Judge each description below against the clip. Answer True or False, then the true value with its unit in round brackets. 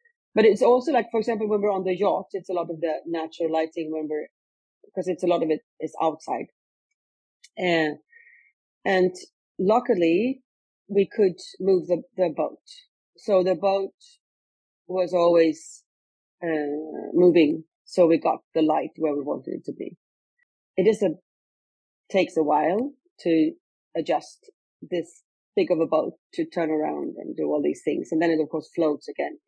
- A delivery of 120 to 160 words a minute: False (170 wpm)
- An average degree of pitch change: True (4.1 semitones)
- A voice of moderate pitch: True (175 Hz)